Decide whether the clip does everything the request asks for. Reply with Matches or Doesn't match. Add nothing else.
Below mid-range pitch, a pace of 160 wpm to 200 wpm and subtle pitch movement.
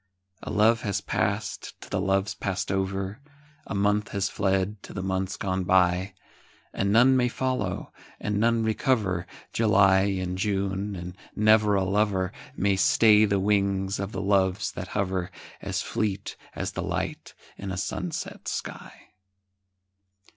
Doesn't match